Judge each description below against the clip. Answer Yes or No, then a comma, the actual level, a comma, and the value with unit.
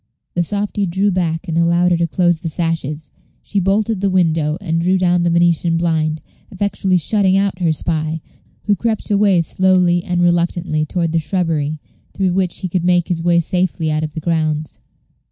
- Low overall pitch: No, medium, 175 Hz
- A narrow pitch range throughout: Yes, narrow, 2.3 semitones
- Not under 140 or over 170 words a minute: No, average, 185 wpm